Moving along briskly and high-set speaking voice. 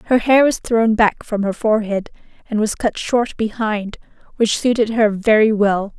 No: average, 180 wpm; high, 220 Hz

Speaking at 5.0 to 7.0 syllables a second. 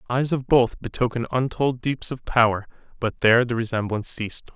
Yes: 5.8 syllables/s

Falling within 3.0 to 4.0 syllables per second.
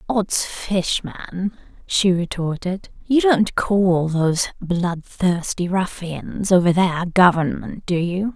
Yes: 3.6 syllables/s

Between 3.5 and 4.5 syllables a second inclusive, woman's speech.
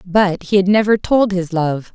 Yes: 4.3 syllables/s; female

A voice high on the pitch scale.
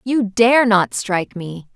Yes: high, 210 Hz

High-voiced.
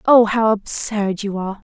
Yes: high, 210 Hz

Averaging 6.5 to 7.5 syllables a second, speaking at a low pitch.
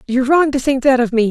No: 6.7 syllables/s; very high, 260 Hz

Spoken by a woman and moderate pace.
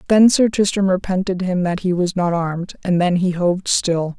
No: female; fast, 215 wpm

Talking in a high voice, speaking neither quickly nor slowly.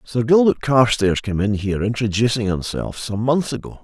No: low, 115 Hz; average, 170 wpm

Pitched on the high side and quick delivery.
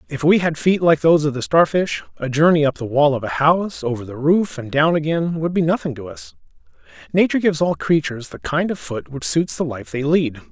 No: medium, 145 Hz; fast, 240 wpm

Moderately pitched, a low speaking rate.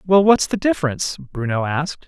No: medium, 160 Hz; average, 175 wpm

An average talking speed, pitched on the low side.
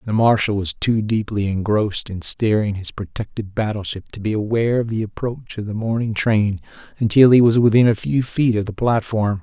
Yes: average, 195 wpm; low, 110 Hz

